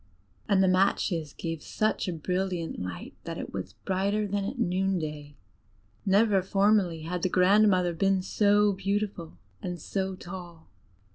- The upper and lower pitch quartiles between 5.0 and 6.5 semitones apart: No, narrow, 2.6 semitones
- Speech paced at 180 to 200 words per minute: No, average, 145 wpm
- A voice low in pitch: No, high, 190 Hz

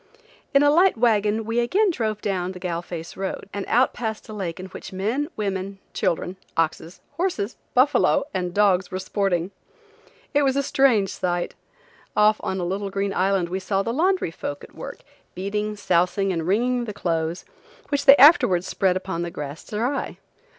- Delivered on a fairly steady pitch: No, average, 4.6 semitones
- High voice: Yes, high, 200 Hz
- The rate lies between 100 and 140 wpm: No, average, 180 wpm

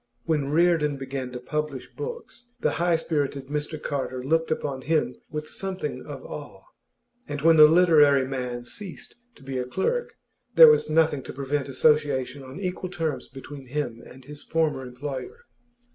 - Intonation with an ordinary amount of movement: Yes, average, 3.5 semitones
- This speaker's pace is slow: No, average, 160 wpm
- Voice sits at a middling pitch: Yes, medium, 145 Hz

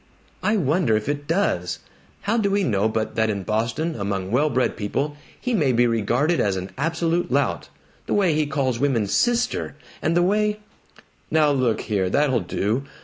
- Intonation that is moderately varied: No, wide, 7.2 semitones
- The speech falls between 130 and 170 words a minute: No, average, 185 wpm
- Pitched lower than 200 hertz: Yes, medium, 140 Hz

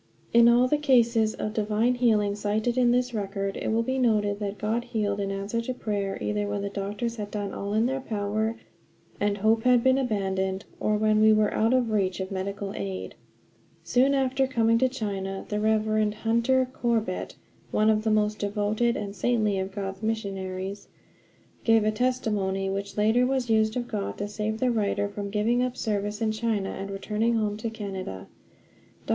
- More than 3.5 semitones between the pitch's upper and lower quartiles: No, narrow, 2.5 semitones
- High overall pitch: Yes, high, 215 Hz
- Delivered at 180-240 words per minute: Yes, average, 185 wpm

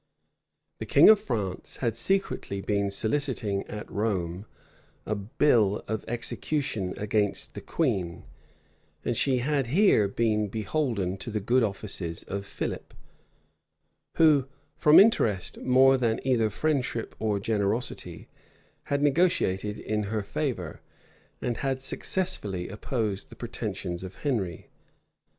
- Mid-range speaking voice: No, low, 110 Hz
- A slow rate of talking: Yes, slow, 120 wpm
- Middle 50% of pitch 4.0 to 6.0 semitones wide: Yes, average, 5.0 semitones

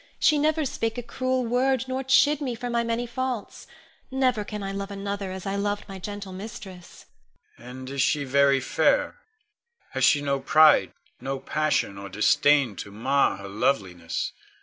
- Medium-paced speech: Yes, average, 170 wpm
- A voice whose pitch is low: No, high, 195 Hz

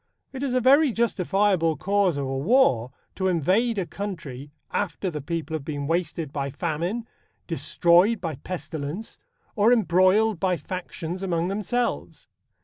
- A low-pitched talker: No, medium, 180 Hz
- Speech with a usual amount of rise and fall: Yes, average, 4.7 semitones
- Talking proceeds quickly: No, average, 140 wpm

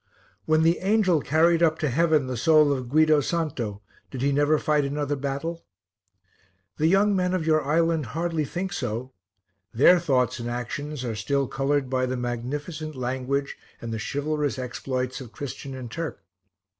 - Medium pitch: Yes, medium, 145 Hz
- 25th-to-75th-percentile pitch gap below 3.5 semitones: No, average, 3.8 semitones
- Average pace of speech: Yes, average, 165 wpm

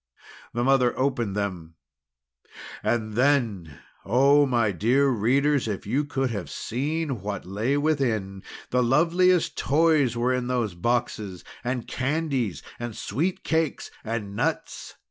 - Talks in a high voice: No, low, 125 Hz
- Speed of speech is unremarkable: No, slow, 125 wpm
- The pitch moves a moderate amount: Yes, average, 4.8 semitones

